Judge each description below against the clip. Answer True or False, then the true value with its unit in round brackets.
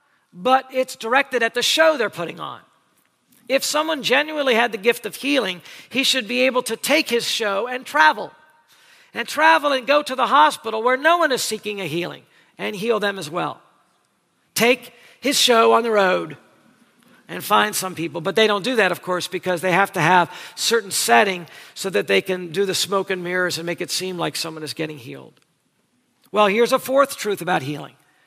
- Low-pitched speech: False (225 Hz)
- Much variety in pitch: True (6.1 semitones)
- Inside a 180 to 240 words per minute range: True (200 wpm)